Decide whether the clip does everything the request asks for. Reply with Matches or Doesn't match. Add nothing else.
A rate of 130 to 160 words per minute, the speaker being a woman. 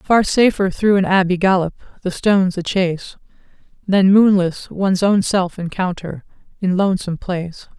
Matches